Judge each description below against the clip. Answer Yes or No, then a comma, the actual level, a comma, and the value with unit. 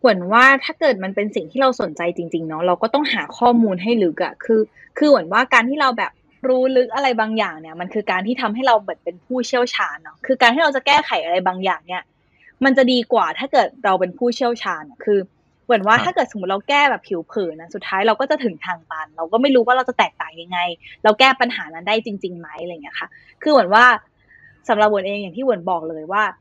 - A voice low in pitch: No, high, 225 Hz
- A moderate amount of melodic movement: No, wide, 5.8 semitones